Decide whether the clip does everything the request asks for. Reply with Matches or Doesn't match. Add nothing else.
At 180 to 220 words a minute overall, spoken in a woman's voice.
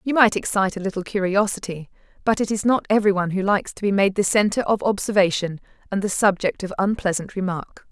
Matches